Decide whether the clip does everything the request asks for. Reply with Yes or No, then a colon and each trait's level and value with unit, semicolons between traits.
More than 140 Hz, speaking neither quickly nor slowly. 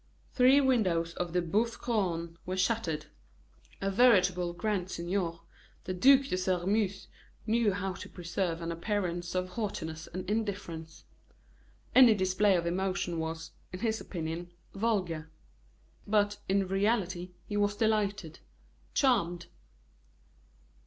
No: medium, 185 Hz; slow, 120 wpm